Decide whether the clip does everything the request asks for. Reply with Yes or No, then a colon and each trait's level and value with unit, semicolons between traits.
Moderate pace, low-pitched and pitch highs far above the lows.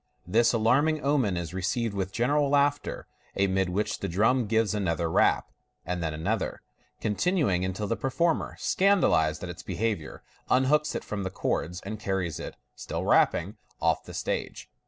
Yes: average, 155 wpm; low, 105 Hz; wide, 6.3 semitones